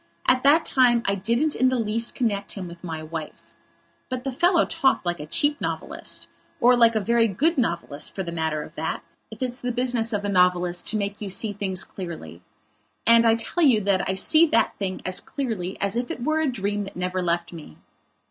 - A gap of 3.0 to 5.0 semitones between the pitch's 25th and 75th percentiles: No, wide, 5.4 semitones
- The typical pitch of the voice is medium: No, high, 210 Hz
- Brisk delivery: Yes, fast, 210 wpm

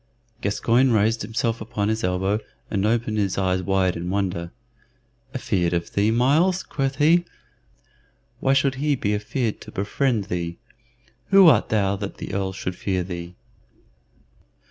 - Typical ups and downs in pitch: Yes, average, 4.9 semitones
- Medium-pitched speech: No, low, 105 Hz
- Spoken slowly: No, average, 145 wpm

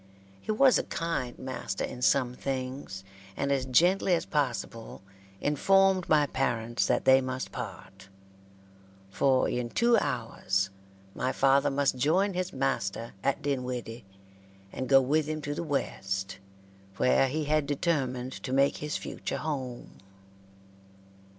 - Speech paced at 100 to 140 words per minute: Yes, slow, 135 wpm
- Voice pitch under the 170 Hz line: Yes, low, 135 Hz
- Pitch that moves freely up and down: No, average, 3.4 semitones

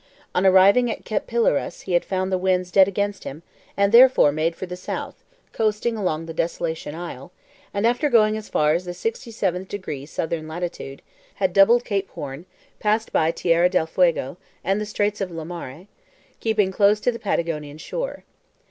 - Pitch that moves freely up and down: No, average, 4.0 semitones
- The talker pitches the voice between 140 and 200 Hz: Yes, medium, 185 Hz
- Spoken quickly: No, average, 180 wpm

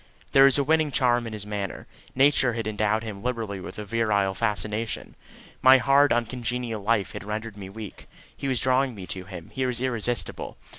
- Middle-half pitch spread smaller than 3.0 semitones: No, average, 3.6 semitones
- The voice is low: Yes, low, 115 Hz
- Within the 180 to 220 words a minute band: Yes, average, 185 wpm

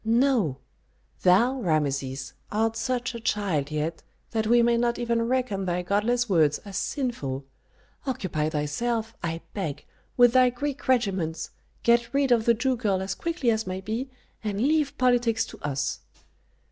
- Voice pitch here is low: No, high, 225 Hz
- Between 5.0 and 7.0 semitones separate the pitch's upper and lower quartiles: Yes, wide, 5.5 semitones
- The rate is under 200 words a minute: Yes, average, 155 wpm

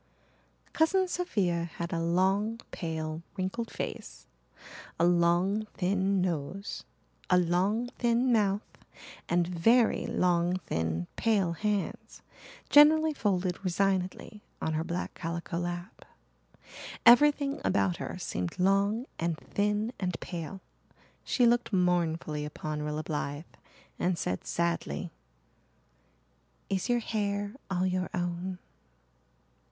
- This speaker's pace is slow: Yes, slow, 110 wpm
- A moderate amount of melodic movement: Yes, average, 3.7 semitones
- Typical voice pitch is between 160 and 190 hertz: Yes, medium, 185 Hz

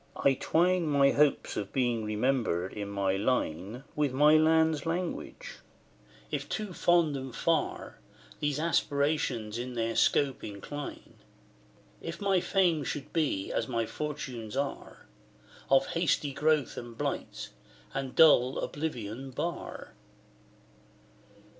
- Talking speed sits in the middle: No, slow, 120 wpm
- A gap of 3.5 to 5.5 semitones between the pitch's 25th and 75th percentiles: Yes, average, 5.1 semitones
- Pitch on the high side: No, medium, 140 Hz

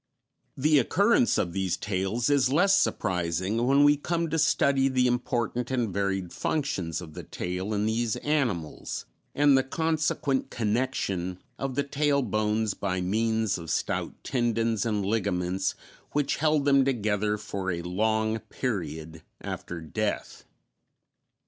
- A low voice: Yes, low, 110 Hz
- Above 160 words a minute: No, slow, 135 wpm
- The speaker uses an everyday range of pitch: No, wide, 6.2 semitones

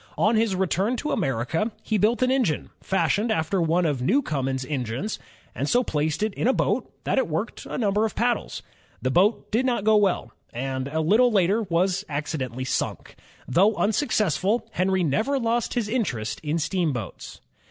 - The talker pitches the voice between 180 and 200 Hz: Yes, high, 190 Hz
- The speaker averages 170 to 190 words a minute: Yes, average, 175 wpm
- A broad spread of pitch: Yes, wide, 6.8 semitones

